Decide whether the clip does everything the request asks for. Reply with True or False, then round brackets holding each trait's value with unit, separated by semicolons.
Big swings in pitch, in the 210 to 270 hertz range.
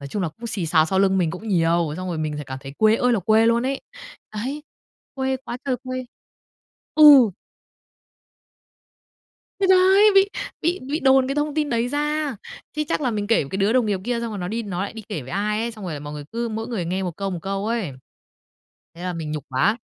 True (6.3 semitones; 215 Hz)